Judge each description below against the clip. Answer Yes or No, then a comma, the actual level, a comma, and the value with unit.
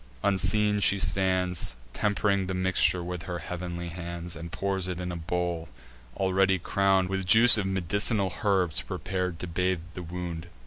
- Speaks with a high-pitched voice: No, very low, 90 Hz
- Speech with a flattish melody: Yes, narrow, 1.8 semitones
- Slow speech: No, average, 160 wpm